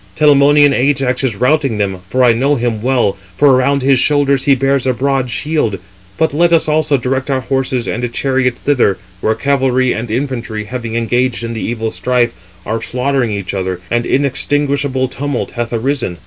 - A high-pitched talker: No, low, 130 Hz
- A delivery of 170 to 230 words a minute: Yes, average, 175 wpm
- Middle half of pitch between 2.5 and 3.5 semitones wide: Yes, average, 3.0 semitones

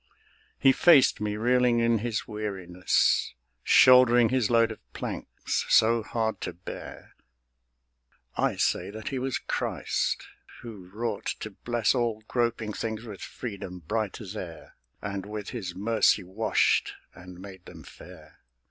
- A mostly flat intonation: No, average, 3.0 semitones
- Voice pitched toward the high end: No, low, 110 Hz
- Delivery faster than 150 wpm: No, average, 140 wpm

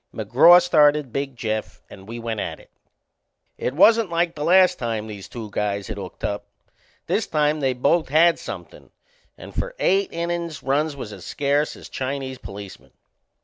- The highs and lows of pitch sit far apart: Yes, wide, 7.3 semitones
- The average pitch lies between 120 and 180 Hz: Yes, medium, 140 Hz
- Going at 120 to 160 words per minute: No, average, 170 wpm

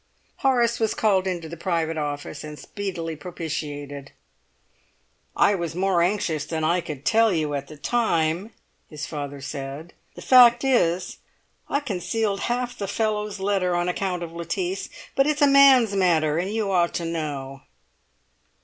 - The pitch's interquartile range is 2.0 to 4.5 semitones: No, wide, 5.4 semitones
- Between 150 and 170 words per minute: Yes, average, 155 wpm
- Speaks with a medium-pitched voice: Yes, medium, 175 Hz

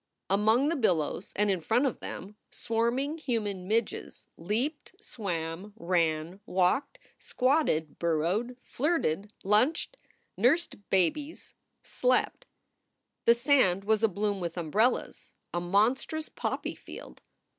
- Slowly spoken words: Yes, slow, 110 wpm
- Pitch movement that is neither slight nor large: No, wide, 6.0 semitones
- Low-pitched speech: No, high, 210 Hz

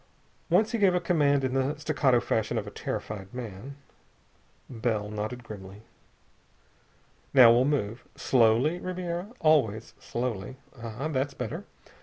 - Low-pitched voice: Yes, low, 125 Hz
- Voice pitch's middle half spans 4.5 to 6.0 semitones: Yes, average, 5.3 semitones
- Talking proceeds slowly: Yes, slow, 130 wpm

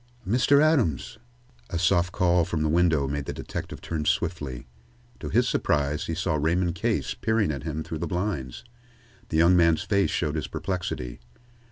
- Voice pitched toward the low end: Yes, very low, 85 Hz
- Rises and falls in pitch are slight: No, average, 3.4 semitones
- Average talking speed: Yes, average, 170 wpm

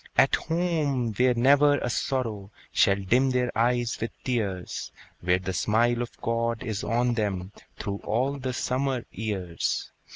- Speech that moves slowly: No, average, 150 wpm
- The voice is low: Yes, low, 120 Hz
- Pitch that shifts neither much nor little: Yes, average, 3.8 semitones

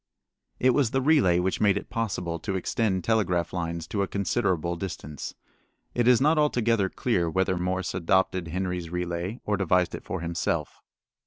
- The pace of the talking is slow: No, average, 165 wpm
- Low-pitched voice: Yes, very low, 95 Hz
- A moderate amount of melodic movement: Yes, average, 4.3 semitones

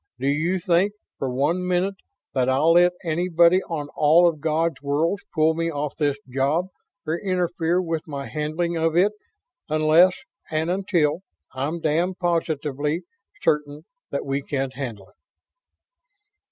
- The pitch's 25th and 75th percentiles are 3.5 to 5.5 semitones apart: No, average, 3.1 semitones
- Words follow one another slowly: No, average, 145 wpm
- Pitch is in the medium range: Yes, medium, 160 Hz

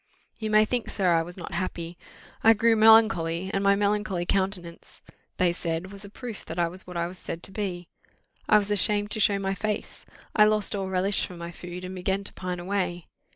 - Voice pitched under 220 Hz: Yes, high, 190 Hz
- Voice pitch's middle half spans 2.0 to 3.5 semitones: Yes, average, 2.9 semitones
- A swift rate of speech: Yes, fast, 215 wpm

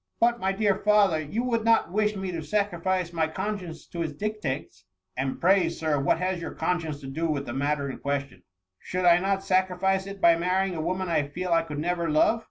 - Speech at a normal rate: No, fast, 245 wpm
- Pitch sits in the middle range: Yes, medium, 175 Hz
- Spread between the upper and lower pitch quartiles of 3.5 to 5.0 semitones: Yes, average, 4.2 semitones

